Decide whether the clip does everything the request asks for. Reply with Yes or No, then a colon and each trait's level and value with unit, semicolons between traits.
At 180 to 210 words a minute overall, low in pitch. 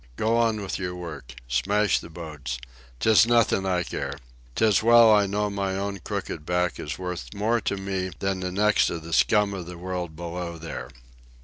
Yes: average, 190 wpm; very low, 95 Hz